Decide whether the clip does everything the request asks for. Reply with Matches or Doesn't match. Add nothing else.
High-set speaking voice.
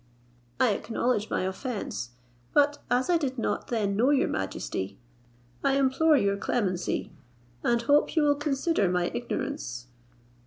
Matches